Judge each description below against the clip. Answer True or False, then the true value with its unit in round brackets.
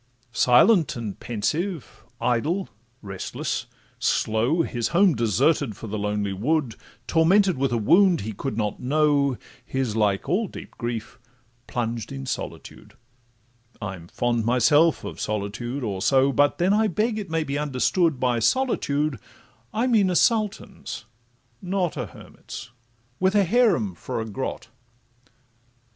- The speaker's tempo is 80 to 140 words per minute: True (135 wpm)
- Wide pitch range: True (7.4 semitones)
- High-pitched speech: False (135 Hz)